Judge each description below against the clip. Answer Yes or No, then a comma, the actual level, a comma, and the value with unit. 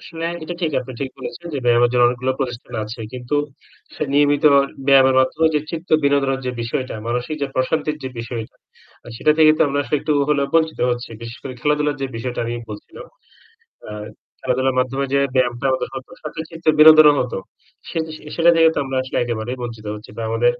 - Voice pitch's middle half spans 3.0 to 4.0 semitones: Yes, average, 3.6 semitones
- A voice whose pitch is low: Yes, low, 130 Hz